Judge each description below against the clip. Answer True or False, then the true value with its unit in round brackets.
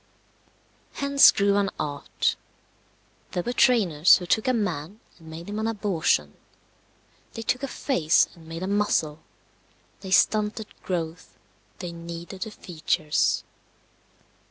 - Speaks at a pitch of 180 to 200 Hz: True (185 Hz)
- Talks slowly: True (130 wpm)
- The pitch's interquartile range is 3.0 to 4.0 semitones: False (4.7 semitones)